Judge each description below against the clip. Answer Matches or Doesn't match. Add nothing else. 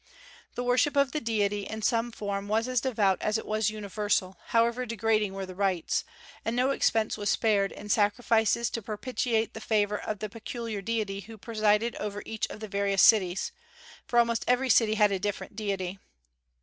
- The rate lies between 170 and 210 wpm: Matches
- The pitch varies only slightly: Matches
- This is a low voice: Doesn't match